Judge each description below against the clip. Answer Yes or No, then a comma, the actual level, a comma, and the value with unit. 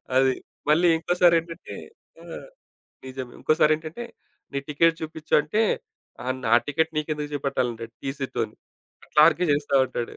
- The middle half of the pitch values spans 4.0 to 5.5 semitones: No, average, 3.3 semitones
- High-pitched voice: No, medium, 150 Hz